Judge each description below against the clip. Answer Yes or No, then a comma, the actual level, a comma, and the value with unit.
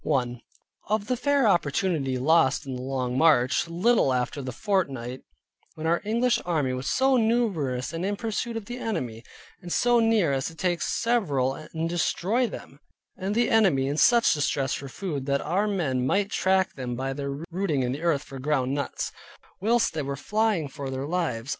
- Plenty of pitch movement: Yes, wide, 7.4 semitones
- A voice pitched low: No, medium, 160 Hz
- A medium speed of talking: Yes, average, 190 wpm